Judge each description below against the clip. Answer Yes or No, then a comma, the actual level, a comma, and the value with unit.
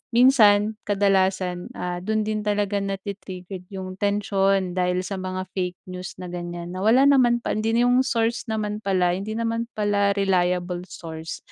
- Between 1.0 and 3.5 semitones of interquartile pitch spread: Yes, average, 2.9 semitones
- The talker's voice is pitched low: No, high, 195 Hz